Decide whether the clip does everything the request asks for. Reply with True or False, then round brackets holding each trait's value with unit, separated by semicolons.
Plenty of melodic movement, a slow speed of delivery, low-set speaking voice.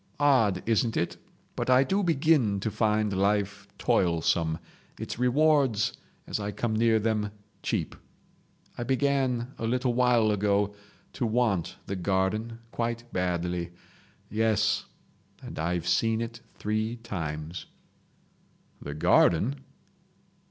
False (4.1 semitones; 115 wpm; 110 Hz)